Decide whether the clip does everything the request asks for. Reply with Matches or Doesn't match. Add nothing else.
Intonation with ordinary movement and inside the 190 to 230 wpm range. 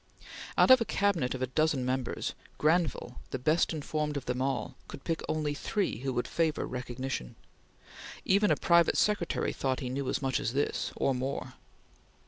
Doesn't match